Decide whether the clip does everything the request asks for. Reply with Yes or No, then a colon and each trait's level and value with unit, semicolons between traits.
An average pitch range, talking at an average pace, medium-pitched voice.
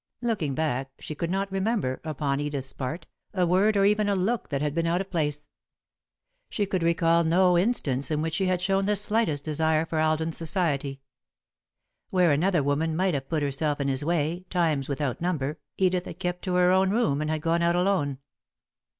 Yes: average, 4.1 semitones; average, 195 wpm; medium, 165 Hz